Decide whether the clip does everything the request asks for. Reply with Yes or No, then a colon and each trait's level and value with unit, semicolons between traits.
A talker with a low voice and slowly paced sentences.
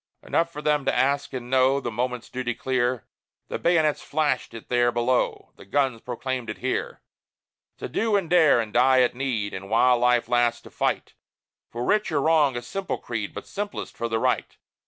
No: low, 125 Hz; average, 195 wpm